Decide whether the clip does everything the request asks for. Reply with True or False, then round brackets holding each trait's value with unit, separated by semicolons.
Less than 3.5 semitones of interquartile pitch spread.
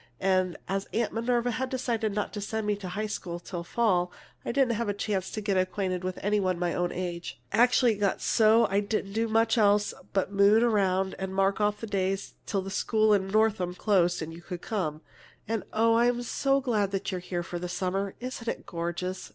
True (3.1 semitones)